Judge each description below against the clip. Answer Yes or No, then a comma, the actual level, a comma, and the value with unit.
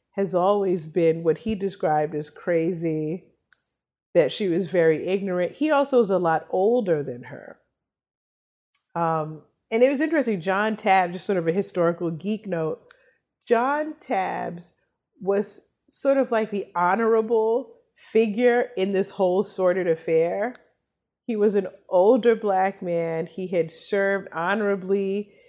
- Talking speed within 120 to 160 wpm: Yes, average, 140 wpm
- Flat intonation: No, average, 4.7 semitones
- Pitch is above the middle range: Yes, high, 195 Hz